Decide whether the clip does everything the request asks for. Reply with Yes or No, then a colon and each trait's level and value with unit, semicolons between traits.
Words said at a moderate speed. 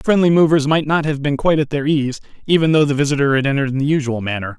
No: fast, 275 wpm